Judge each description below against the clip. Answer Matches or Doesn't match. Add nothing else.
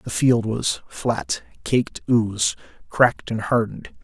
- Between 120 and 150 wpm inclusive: Matches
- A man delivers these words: Matches